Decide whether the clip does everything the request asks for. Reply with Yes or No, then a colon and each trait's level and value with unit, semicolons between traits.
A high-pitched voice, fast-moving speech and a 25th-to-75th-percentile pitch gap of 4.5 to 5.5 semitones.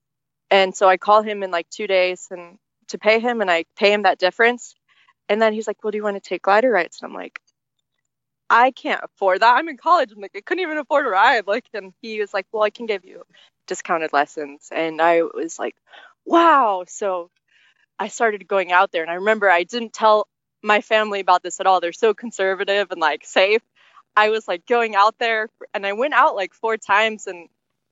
No: high, 205 Hz; fast, 225 wpm; average, 3.5 semitones